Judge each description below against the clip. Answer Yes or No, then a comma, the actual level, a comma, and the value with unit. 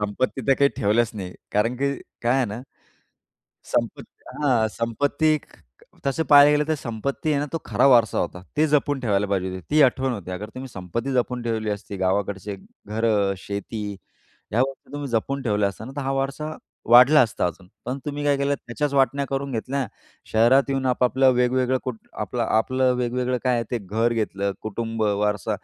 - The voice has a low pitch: Yes, low, 125 Hz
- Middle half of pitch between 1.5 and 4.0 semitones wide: No, average, 4.5 semitones